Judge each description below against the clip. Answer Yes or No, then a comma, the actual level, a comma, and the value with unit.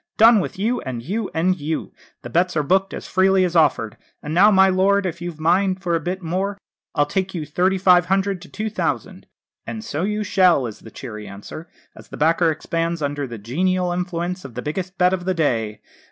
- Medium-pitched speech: Yes, medium, 180 Hz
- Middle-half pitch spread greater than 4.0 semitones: No, average, 3.7 semitones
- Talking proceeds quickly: Yes, fast, 220 wpm